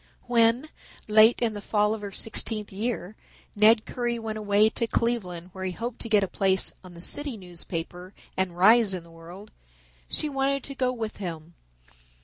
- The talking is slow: No, average, 180 wpm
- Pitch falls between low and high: No, high, 215 Hz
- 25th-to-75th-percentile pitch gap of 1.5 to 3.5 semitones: No, average, 4.0 semitones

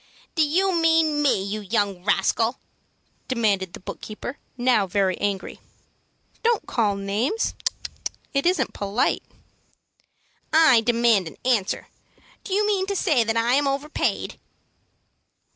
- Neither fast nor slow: No, slow, 125 wpm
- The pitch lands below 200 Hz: No, high, 240 Hz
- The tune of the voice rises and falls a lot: Yes, wide, 7.4 semitones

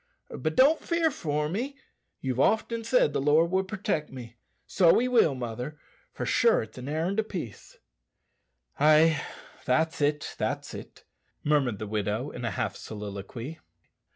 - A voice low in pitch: No, medium, 150 Hz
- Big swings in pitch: Yes, wide, 7.4 semitones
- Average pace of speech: Yes, average, 155 wpm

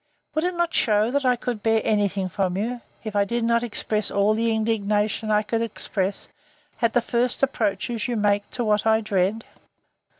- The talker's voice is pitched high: Yes, high, 220 Hz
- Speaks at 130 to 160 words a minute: No, average, 195 wpm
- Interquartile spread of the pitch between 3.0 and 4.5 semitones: No, narrow, 2.4 semitones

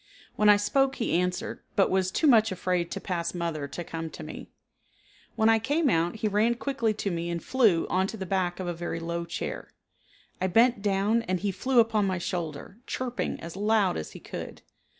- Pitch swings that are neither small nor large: Yes, average, 4.4 semitones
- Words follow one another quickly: Yes, fast, 210 wpm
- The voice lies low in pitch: No, high, 190 Hz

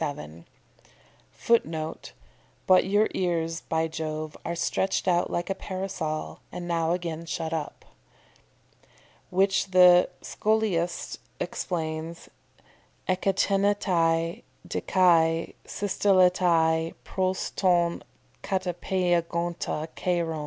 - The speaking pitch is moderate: Yes, medium, 175 Hz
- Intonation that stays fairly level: Yes, narrow, 2.3 semitones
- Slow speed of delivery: Yes, slow, 85 wpm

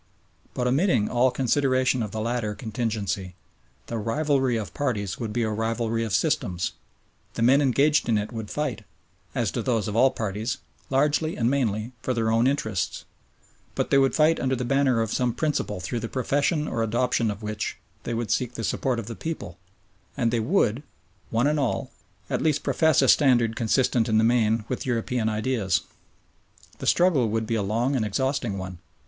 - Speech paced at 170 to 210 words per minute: Yes, average, 185 wpm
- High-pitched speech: No, low, 120 Hz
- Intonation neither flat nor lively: Yes, average, 3.3 semitones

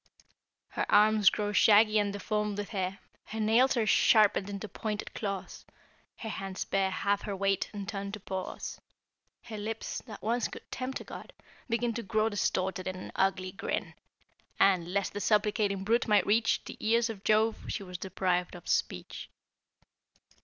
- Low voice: No, high, 205 Hz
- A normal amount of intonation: No, narrow, 2.0 semitones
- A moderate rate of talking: Yes, average, 165 wpm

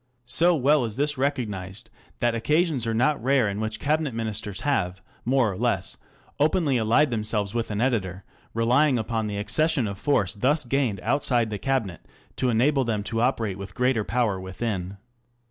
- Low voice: Yes, low, 115 Hz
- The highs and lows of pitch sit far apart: No, average, 4.7 semitones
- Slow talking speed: No, average, 170 wpm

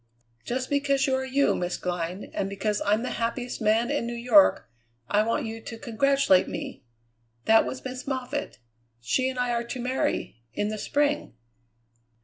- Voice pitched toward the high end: Yes, high, 240 Hz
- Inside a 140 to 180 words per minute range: Yes, average, 170 wpm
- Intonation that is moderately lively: Yes, average, 3.5 semitones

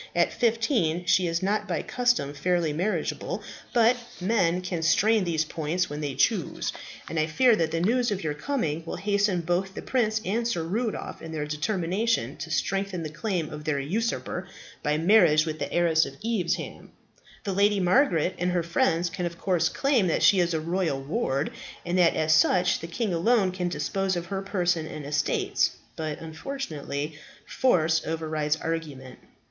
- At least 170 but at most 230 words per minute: Yes, average, 175 wpm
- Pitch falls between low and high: Yes, medium, 175 Hz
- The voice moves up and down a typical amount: Yes, average, 4.2 semitones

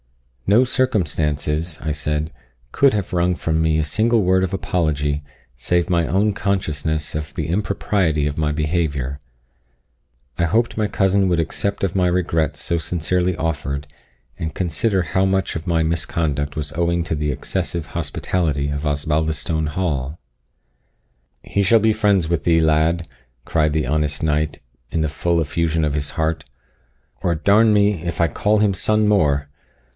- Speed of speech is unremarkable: Yes, average, 160 wpm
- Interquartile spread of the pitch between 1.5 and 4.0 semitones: Yes, average, 3.6 semitones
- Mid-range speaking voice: No, very low, 80 Hz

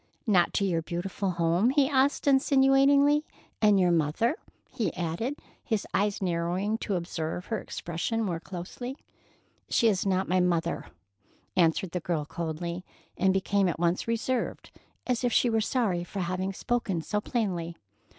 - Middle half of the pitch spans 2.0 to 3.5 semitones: No, average, 5.1 semitones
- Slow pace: No, average, 150 wpm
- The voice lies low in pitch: No, high, 190 Hz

